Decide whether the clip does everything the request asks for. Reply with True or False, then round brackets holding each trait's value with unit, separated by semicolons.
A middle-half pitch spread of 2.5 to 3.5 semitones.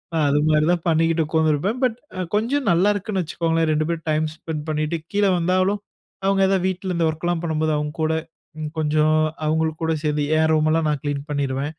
True (2.8 semitones)